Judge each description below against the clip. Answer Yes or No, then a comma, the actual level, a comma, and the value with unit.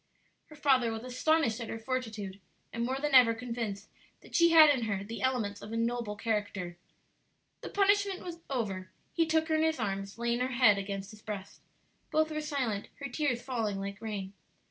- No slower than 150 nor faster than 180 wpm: No, average, 190 wpm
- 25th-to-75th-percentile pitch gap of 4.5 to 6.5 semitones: Yes, average, 5.2 semitones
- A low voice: No, high, 235 Hz